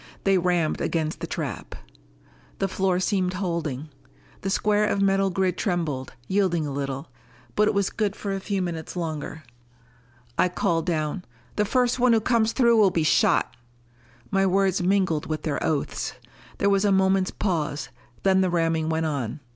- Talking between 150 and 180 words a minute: Yes, average, 170 wpm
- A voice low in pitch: No, medium, 185 Hz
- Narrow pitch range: No, average, 3.7 semitones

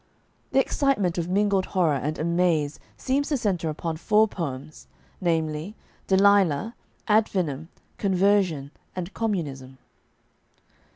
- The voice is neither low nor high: Yes, medium, 180 Hz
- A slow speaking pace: Yes, slow, 110 wpm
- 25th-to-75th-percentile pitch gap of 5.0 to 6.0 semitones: No, average, 4.6 semitones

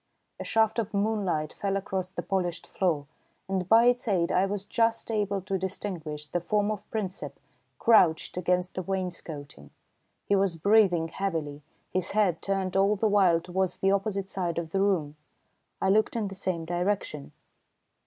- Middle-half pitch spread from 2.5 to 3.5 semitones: Yes, average, 2.8 semitones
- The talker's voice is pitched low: No, high, 190 Hz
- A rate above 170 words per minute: No, average, 165 wpm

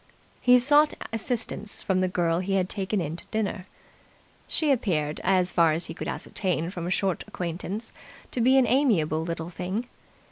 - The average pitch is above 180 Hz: Yes, high, 190 Hz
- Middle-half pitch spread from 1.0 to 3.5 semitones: No, average, 4.9 semitones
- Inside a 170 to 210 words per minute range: Yes, average, 175 wpm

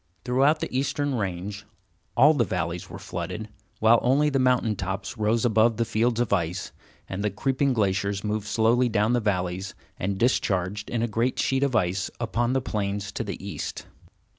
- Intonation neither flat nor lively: Yes, average, 3.8 semitones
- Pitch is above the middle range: No, low, 110 Hz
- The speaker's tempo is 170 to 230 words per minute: Yes, average, 180 wpm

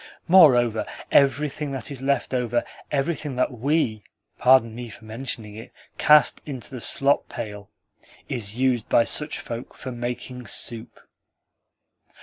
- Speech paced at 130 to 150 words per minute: Yes, slow, 135 wpm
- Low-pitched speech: Yes, low, 125 Hz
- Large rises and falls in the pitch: No, average, 3.1 semitones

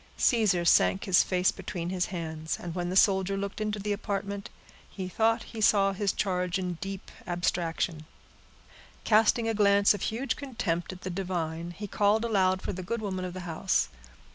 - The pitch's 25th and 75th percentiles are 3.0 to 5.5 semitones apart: No, narrow, 2.6 semitones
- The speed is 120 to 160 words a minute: No, average, 180 wpm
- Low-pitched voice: No, high, 190 Hz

